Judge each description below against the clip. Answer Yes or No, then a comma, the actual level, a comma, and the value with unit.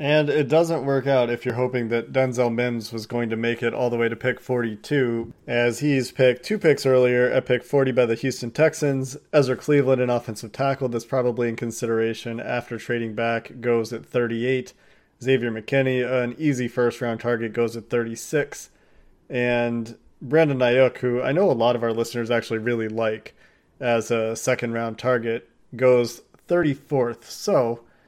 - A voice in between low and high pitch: No, low, 120 Hz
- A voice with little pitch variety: Yes, narrow, 2.0 semitones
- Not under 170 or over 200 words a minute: Yes, average, 175 wpm